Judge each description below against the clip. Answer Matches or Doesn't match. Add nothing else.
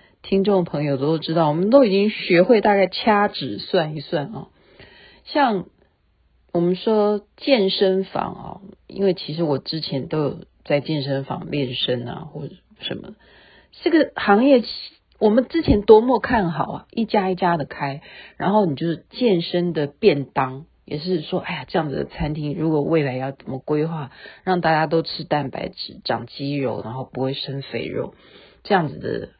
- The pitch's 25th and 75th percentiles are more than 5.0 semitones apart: Matches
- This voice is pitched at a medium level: Matches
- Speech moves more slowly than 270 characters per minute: Matches